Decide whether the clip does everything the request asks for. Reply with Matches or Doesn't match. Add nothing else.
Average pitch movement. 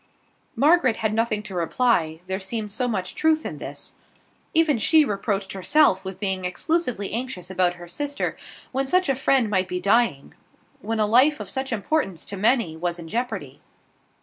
Doesn't match